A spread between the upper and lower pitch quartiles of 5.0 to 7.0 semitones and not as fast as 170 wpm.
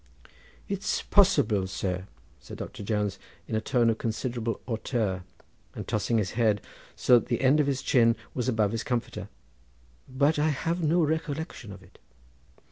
Yes: average, 5.3 semitones; average, 160 wpm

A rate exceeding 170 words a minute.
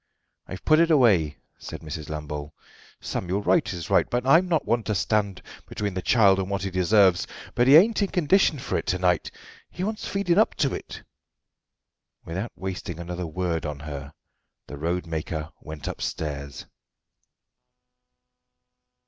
No: average, 155 wpm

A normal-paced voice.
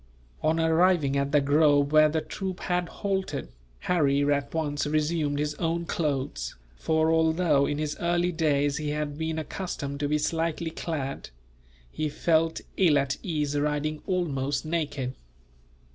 Yes: average, 145 wpm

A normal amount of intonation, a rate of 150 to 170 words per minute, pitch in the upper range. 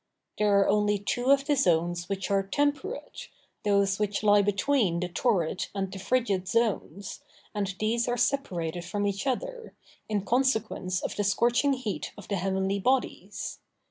Yes: average, 4.1 semitones; average, 160 wpm; high, 205 Hz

